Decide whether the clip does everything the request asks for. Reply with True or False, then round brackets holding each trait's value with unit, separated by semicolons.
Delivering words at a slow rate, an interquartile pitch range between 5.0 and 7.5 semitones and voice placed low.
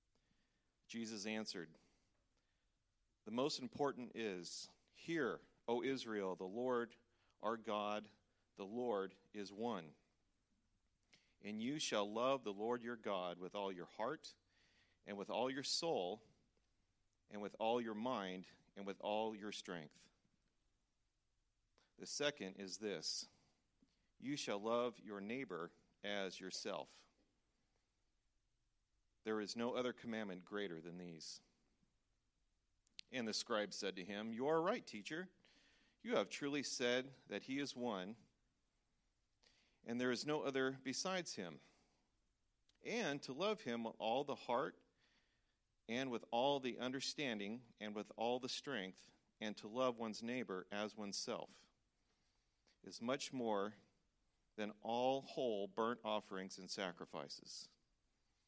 False (125 wpm; 3.8 semitones; 110 Hz)